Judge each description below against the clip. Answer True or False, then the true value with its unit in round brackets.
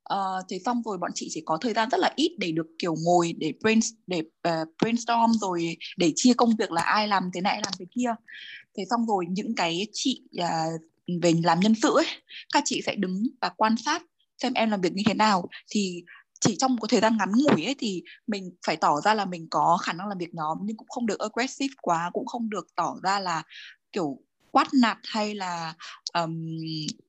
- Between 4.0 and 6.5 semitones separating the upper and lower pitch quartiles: True (5.2 semitones)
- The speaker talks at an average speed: True (225 wpm)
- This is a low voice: False (205 Hz)